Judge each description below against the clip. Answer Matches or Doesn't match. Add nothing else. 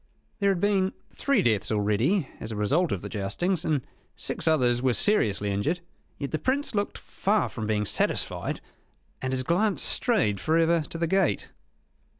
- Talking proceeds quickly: Doesn't match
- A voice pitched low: Doesn't match